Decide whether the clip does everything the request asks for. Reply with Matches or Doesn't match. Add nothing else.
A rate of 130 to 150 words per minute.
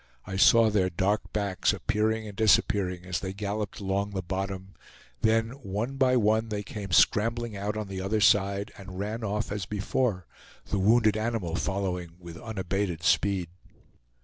Doesn't match